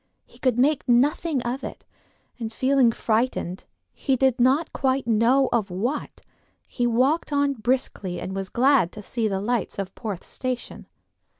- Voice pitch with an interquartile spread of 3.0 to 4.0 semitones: Yes, average, 3.6 semitones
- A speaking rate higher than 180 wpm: No, average, 160 wpm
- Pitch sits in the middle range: No, high, 245 Hz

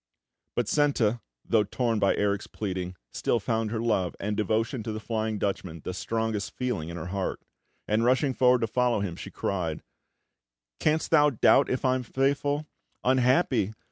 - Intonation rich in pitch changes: No, average, 4.1 semitones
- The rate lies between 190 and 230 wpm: No, average, 170 wpm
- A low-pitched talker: Yes, low, 110 Hz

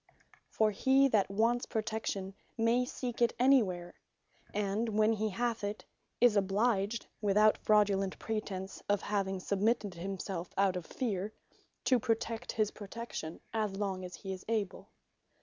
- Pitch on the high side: Yes, high, 210 Hz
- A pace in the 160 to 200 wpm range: No, average, 140 wpm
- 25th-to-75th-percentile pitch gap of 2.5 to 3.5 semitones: Yes, average, 2.8 semitones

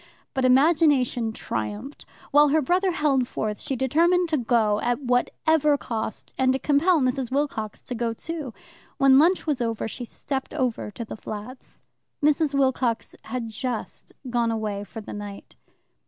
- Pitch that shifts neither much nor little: Yes, average, 4.4 semitones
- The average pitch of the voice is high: Yes, very high, 255 Hz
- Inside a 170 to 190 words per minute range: No, average, 155 wpm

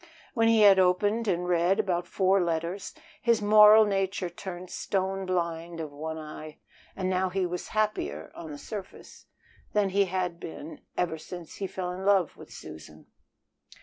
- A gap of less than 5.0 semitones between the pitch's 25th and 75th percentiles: Yes, average, 2.7 semitones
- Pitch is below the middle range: No, medium, 185 Hz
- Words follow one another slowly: No, average, 165 wpm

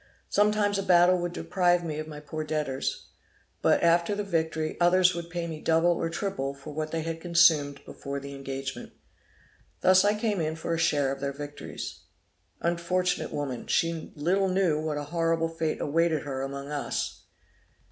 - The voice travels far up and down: No, average, 3.0 semitones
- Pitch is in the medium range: Yes, medium, 165 Hz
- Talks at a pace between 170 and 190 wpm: Yes, average, 175 wpm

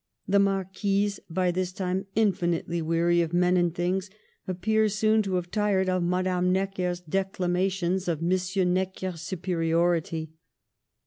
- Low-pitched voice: No, medium, 185 Hz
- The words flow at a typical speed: No, slow, 130 wpm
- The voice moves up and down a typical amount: No, narrow, 1.8 semitones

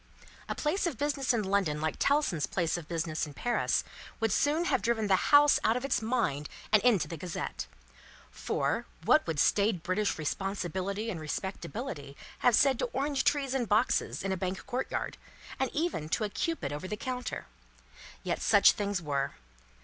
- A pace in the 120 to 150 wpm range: No, average, 175 wpm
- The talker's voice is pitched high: Yes, high, 205 Hz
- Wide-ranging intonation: Yes, wide, 7.0 semitones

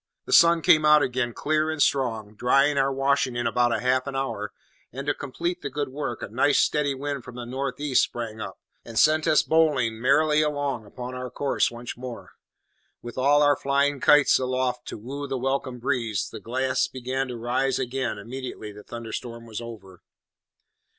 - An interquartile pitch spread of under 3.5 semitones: Yes, average, 3.0 semitones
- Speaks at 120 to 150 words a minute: No, average, 185 wpm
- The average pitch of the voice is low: Yes, low, 130 Hz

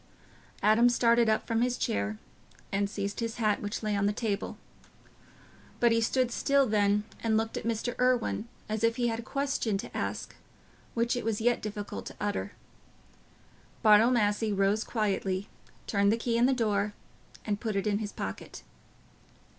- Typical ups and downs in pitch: No, narrow, 2.3 semitones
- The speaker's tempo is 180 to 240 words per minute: No, average, 170 wpm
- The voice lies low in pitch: No, high, 220 Hz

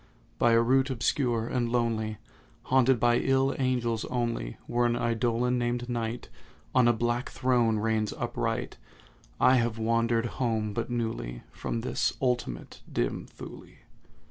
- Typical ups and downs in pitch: No, narrow, 1.5 semitones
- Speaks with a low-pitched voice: Yes, low, 120 Hz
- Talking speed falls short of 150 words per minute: Yes, average, 140 wpm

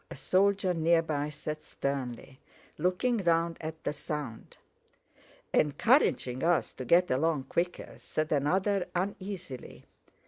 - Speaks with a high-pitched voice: No, medium, 165 Hz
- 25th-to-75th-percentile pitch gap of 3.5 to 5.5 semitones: Yes, average, 4.0 semitones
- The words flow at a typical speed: No, slow, 115 wpm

